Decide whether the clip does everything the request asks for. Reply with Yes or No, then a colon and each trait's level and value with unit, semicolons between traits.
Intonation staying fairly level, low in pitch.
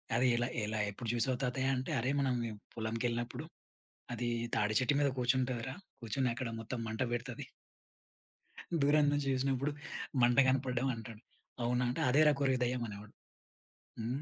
Yes: narrow, 2.2 semitones; low, 125 Hz